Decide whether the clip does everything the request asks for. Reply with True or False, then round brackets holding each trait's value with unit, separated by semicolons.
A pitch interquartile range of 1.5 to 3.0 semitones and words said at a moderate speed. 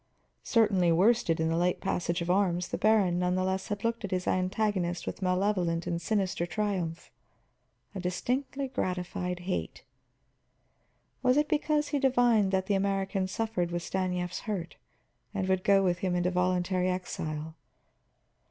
True (2.7 semitones; 145 wpm)